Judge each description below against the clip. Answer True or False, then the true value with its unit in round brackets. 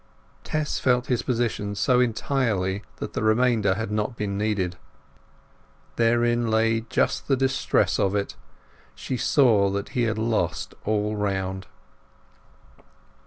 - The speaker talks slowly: True (125 wpm)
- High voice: False (110 Hz)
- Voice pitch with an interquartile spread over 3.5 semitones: False (3.2 semitones)